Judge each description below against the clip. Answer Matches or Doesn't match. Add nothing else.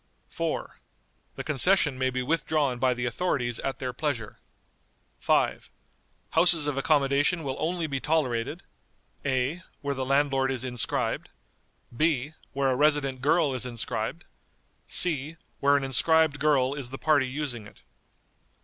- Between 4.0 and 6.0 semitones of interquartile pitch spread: Doesn't match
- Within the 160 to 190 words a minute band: Doesn't match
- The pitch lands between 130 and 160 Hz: Matches